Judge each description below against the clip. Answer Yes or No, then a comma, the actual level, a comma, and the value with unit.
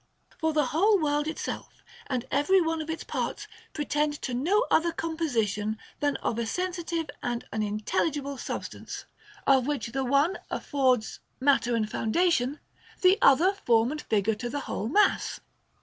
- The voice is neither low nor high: No, very high, 285 Hz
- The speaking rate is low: No, average, 160 wpm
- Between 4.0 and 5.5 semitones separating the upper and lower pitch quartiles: Yes, average, 5.1 semitones